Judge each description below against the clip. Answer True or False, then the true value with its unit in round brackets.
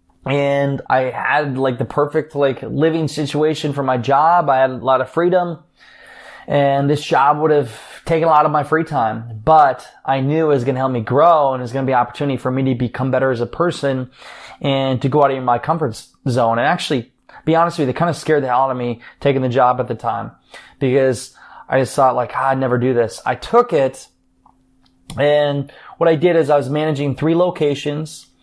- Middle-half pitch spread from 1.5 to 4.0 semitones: True (2.8 semitones)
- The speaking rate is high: True (230 wpm)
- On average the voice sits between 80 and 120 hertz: False (140 Hz)